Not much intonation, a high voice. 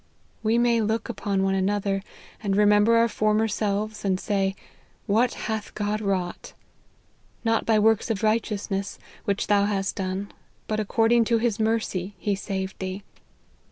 Yes: narrow, 2.1 semitones; high, 210 Hz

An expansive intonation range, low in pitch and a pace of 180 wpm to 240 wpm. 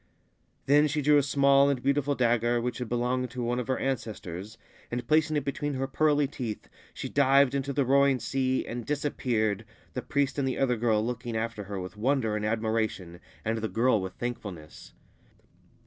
No: average, 3.8 semitones; low, 125 Hz; average, 185 wpm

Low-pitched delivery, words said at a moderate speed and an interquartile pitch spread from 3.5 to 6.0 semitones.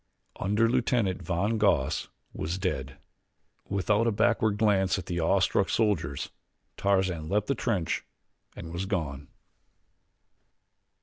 No: very low, 95 Hz; slow, 115 wpm; average, 3.8 semitones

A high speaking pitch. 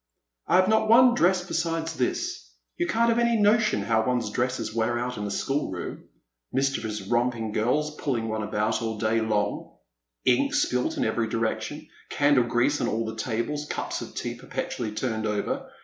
No: low, 120 Hz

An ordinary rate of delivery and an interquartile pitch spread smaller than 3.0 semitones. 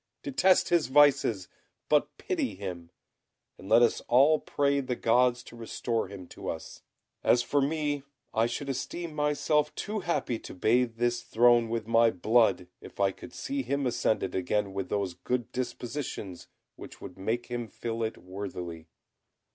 No: average, 165 wpm; wide, 5.6 semitones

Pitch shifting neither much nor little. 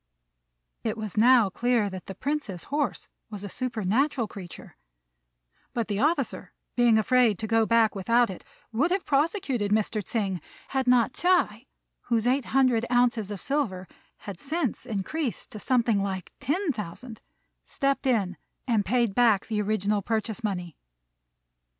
Yes: average, 3.8 semitones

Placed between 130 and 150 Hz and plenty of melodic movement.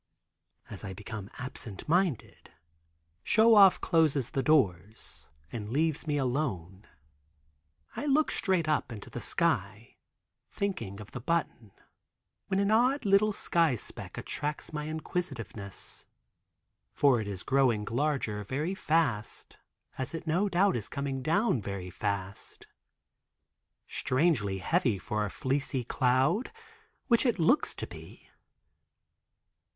Yes: medium, 140 Hz; wide, 8.0 semitones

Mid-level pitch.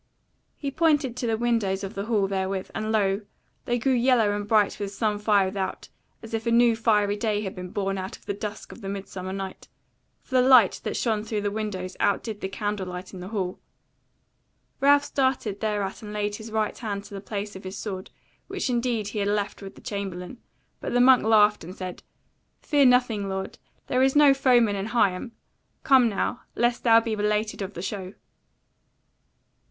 No: high, 210 Hz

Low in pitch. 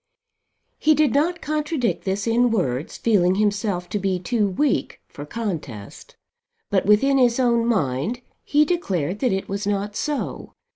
No: high, 210 Hz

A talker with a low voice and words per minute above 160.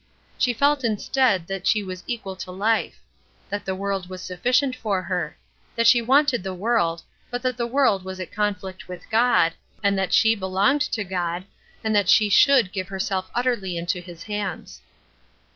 No: high, 200 Hz; average, 175 wpm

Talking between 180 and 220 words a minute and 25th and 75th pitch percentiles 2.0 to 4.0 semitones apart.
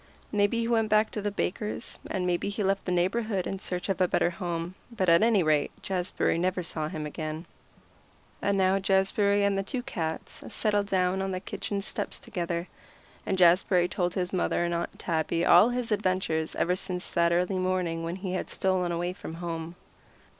Yes: average, 190 wpm; narrow, 2.6 semitones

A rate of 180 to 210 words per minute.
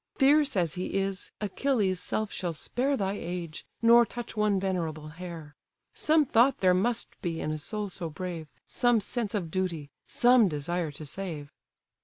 No: average, 165 wpm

